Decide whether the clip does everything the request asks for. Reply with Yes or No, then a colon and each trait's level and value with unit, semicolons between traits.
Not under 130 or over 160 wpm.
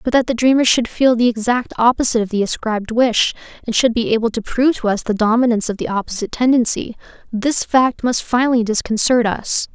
No: average, 195 wpm